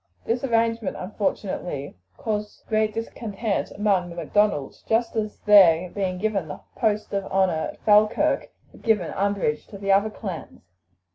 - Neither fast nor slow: Yes, average, 145 wpm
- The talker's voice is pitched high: Yes, high, 205 Hz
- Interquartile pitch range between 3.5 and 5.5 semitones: No, average, 2.9 semitones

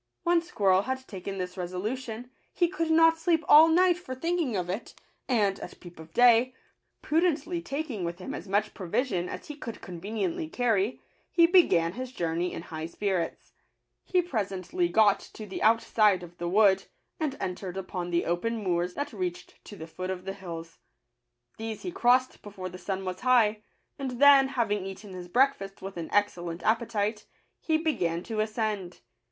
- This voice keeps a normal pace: Yes, average, 180 wpm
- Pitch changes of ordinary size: No, wide, 6.0 semitones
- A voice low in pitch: No, high, 210 Hz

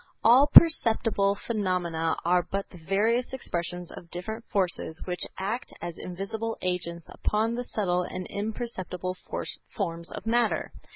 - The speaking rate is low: Yes, slow, 130 wpm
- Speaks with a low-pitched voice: No, high, 195 Hz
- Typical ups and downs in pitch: Yes, average, 4.1 semitones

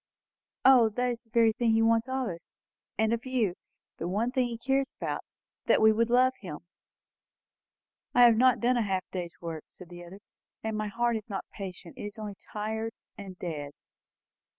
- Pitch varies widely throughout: No, average, 3.8 semitones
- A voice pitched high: Yes, high, 220 Hz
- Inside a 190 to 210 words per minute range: Yes, average, 195 wpm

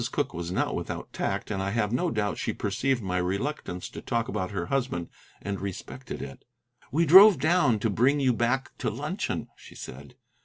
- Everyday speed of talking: Yes, average, 190 wpm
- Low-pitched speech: Yes, low, 115 Hz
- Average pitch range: No, wide, 6.0 semitones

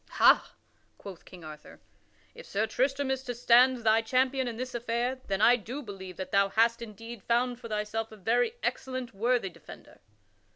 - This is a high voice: Yes, high, 235 Hz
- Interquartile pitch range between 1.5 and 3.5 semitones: Yes, average, 3.2 semitones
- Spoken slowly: No, average, 175 wpm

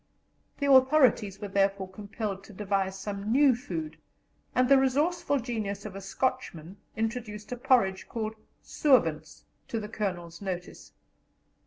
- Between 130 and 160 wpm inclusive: Yes, slow, 135 wpm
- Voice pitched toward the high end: Yes, high, 210 Hz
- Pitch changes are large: No, average, 4.6 semitones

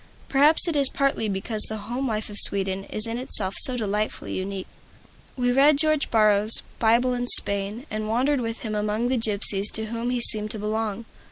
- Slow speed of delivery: No, average, 190 wpm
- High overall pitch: Yes, high, 220 Hz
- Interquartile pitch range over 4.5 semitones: No, average, 3.0 semitones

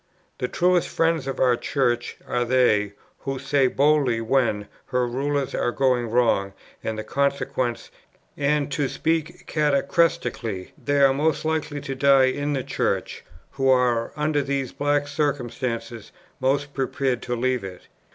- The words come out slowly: No, average, 145 wpm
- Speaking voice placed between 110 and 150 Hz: Yes, low, 135 Hz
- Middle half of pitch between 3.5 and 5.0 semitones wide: No, average, 2.9 semitones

